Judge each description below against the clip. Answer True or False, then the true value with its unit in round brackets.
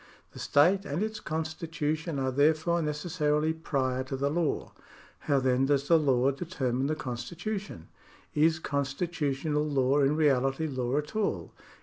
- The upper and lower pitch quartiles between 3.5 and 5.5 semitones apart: False (3.0 semitones)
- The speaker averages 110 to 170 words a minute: True (145 wpm)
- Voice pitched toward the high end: False (150 Hz)